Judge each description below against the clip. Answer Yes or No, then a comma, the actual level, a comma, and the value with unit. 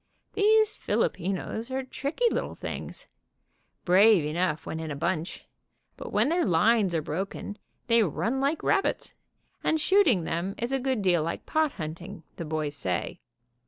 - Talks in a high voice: Yes, high, 195 Hz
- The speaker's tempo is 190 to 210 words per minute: No, average, 155 wpm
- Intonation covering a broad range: Yes, wide, 8.5 semitones